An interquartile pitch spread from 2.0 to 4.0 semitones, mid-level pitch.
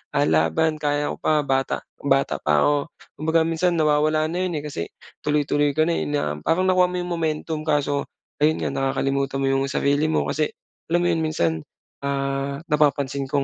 Yes: narrow, 2.4 semitones; medium, 150 Hz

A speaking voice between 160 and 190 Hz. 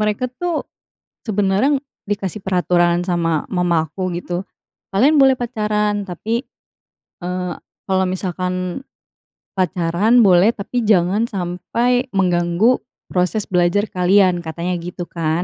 Yes: medium, 185 Hz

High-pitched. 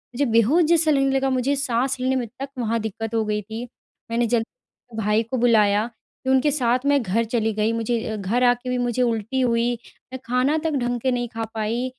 Yes: high, 240 Hz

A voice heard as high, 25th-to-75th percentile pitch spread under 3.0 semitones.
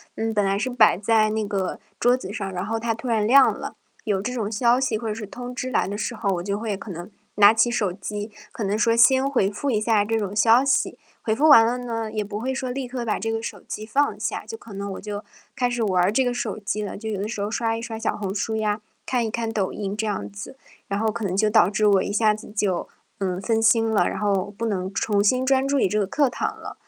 Yes: high, 215 Hz; narrow, 2.6 semitones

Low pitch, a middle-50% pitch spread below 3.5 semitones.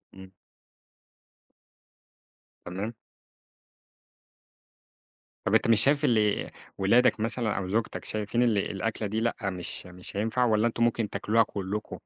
Yes: low, 110 Hz; average, 2.7 semitones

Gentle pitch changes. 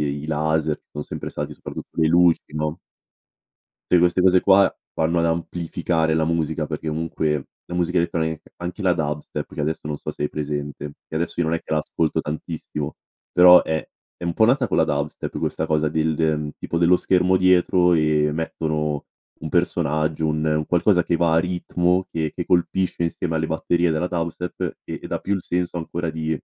Yes: narrow, 2.2 semitones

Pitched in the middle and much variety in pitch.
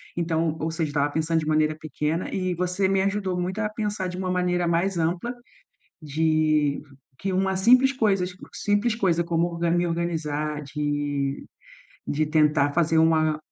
No: medium, 170 Hz; average, 3.2 semitones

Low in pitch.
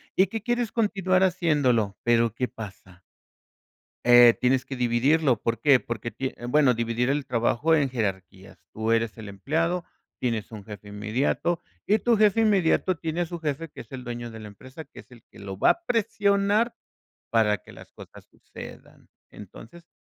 Yes: low, 125 Hz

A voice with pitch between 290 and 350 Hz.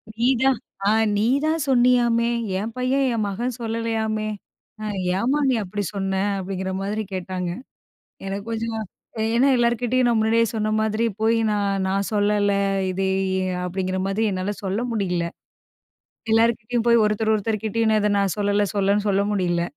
No: high, 215 Hz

